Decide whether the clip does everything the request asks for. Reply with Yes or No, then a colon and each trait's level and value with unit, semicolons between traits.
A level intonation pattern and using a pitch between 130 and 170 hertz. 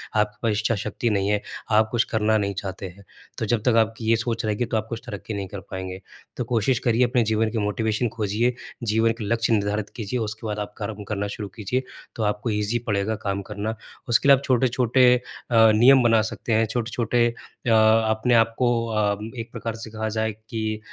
No: narrow, 1.8 semitones; low, 110 Hz